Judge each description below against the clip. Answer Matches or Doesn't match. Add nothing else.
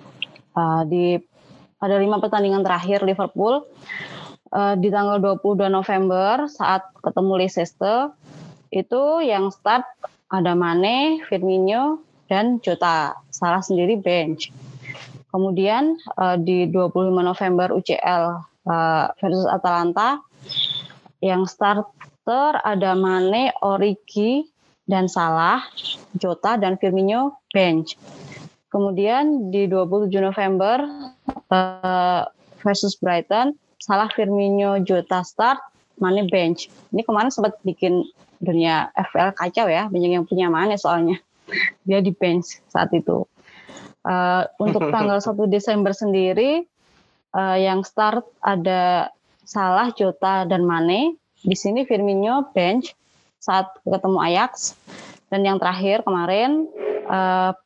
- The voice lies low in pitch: Doesn't match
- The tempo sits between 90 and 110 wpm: Matches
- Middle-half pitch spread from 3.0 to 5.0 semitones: Doesn't match